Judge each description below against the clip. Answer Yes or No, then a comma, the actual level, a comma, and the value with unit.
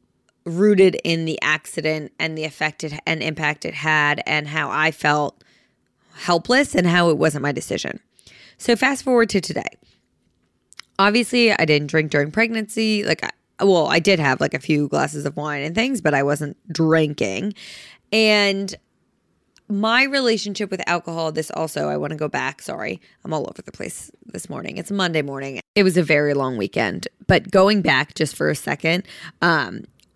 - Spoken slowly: No, average, 175 wpm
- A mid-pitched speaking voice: Yes, medium, 160 Hz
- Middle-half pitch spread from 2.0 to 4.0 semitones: No, average, 5.2 semitones